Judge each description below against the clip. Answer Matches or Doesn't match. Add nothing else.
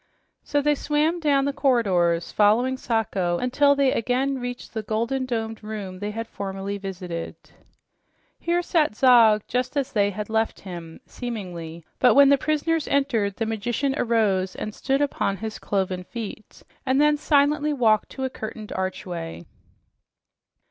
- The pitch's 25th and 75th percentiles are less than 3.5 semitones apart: Doesn't match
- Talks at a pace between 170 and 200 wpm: Doesn't match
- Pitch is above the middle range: Matches